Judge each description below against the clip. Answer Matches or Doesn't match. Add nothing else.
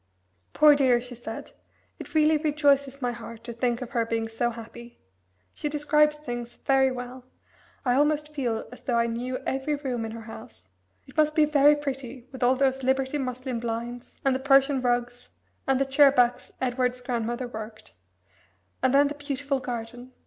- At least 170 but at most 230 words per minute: Matches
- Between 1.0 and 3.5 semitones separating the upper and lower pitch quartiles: Matches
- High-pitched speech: Matches